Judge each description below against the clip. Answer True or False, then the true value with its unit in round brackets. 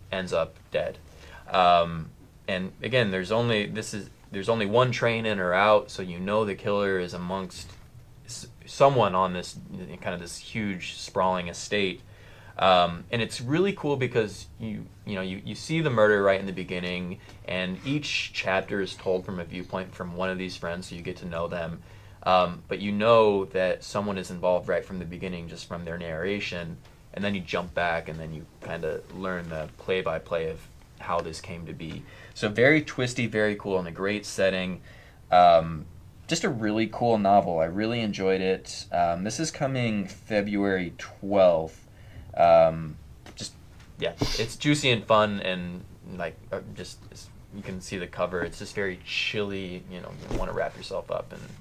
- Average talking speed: True (185 wpm)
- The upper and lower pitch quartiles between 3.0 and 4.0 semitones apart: True (3.3 semitones)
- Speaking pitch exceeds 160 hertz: False (95 Hz)